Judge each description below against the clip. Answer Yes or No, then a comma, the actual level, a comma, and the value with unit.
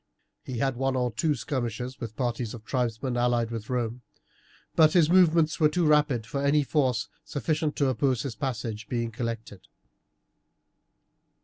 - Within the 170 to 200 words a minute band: No, average, 150 wpm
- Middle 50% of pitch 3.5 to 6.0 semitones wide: Yes, average, 4.0 semitones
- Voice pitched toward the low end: Yes, low, 125 Hz